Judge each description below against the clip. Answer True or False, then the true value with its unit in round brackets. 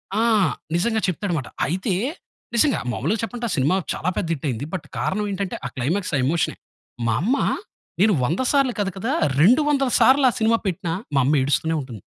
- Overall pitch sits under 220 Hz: True (190 Hz)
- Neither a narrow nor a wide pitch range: False (6.8 semitones)